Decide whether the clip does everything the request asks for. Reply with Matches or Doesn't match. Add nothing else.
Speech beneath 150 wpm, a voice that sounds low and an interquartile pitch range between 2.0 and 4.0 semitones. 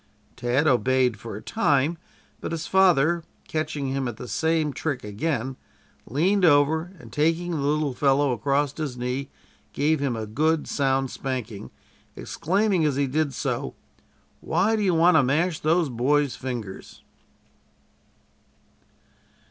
Doesn't match